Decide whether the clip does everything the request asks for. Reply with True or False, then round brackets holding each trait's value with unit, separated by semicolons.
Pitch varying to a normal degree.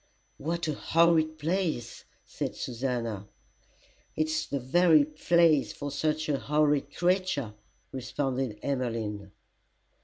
True (3.9 semitones)